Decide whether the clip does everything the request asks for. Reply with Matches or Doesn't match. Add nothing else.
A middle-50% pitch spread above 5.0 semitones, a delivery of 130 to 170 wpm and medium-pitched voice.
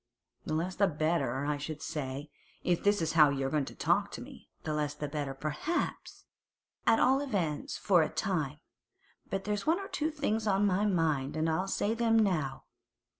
Doesn't match